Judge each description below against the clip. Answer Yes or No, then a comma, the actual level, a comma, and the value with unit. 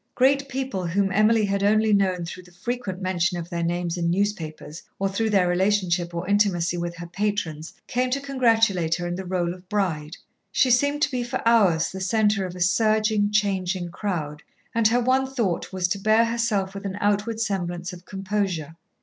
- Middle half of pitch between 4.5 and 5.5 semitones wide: No, average, 3.7 semitones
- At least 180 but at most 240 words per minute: Yes, average, 190 wpm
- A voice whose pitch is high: Yes, high, 195 Hz